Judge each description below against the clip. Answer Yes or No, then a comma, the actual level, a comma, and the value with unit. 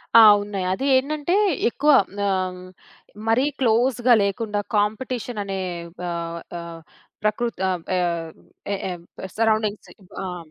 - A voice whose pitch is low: No, high, 205 Hz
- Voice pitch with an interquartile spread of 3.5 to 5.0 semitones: Yes, average, 4.7 semitones